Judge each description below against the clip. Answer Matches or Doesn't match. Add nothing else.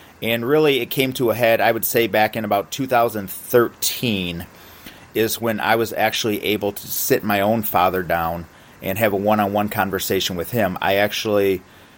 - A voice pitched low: Matches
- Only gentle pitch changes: Doesn't match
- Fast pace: Doesn't match